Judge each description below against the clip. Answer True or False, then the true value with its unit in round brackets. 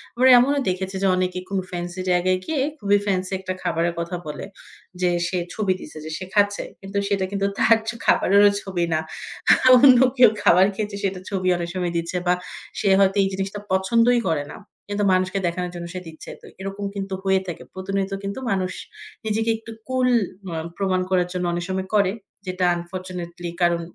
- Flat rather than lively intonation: True (2.0 semitones)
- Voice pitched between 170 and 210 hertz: True (190 Hz)